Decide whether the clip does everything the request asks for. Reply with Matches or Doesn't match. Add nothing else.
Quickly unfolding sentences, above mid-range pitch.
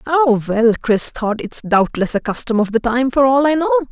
Matches